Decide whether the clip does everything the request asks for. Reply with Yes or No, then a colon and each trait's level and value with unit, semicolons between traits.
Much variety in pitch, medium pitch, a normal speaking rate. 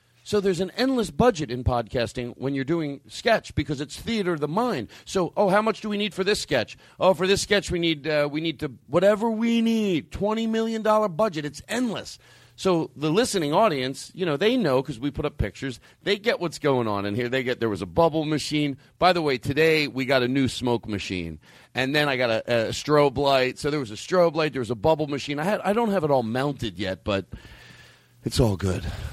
No: wide, 7.3 semitones; medium, 150 Hz; fast, 235 wpm